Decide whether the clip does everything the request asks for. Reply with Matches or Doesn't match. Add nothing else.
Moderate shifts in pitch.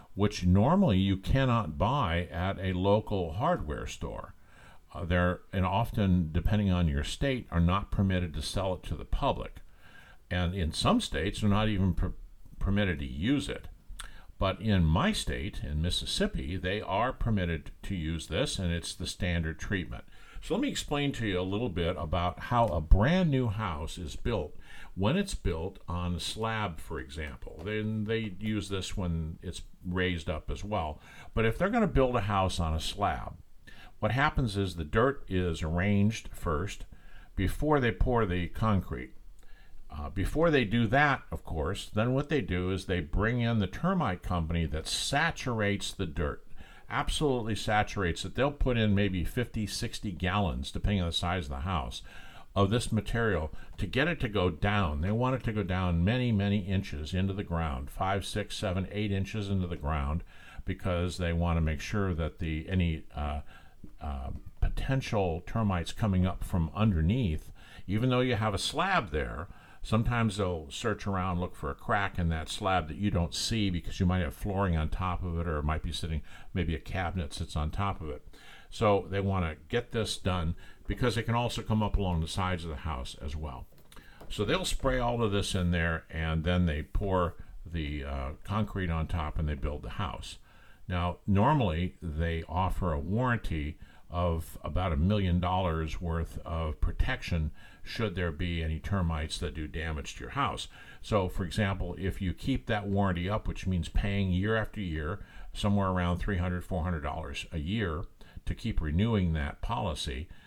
Matches